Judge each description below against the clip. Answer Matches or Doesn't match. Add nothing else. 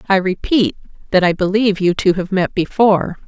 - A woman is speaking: Matches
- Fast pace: Doesn't match